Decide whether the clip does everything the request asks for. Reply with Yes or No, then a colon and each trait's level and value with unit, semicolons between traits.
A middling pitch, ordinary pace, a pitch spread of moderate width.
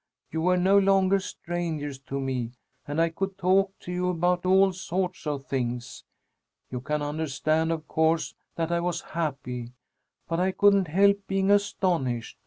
Yes: medium, 170 Hz; average, 160 wpm; average, 4.4 semitones